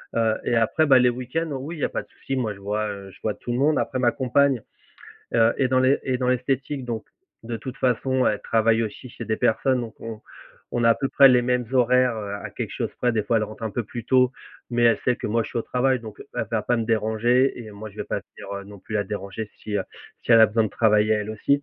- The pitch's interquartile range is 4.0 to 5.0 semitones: No, average, 2.8 semitones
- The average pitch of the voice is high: No, low, 115 Hz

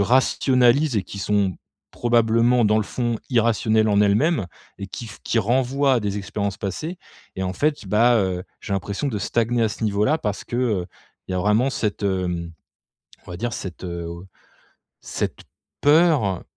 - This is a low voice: Yes, low, 110 Hz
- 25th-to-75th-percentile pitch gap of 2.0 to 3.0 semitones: No, average, 3.7 semitones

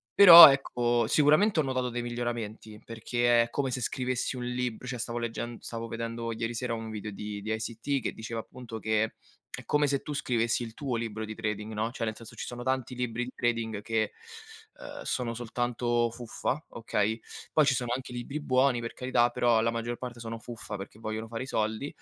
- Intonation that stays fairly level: Yes, narrow, 2.0 semitones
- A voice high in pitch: No, low, 120 Hz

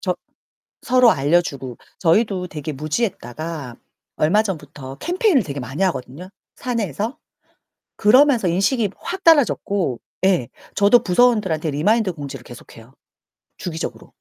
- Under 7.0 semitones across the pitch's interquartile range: No, wide, 7.8 semitones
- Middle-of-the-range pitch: Yes, medium, 180 Hz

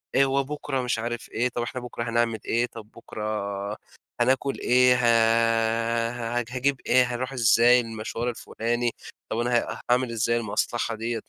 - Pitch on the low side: Yes, low, 120 Hz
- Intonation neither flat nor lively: No, narrow, 1.5 semitones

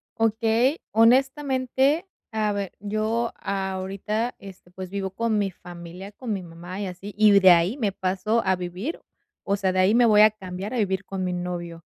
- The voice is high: Yes, high, 200 Hz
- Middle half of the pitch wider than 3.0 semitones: Yes, average, 3.4 semitones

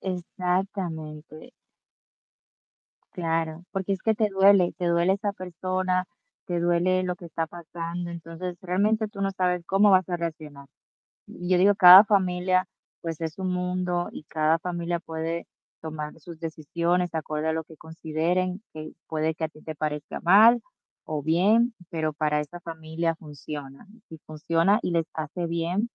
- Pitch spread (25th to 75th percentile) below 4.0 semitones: Yes, narrow, 2.5 semitones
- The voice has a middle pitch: Yes, medium, 170 Hz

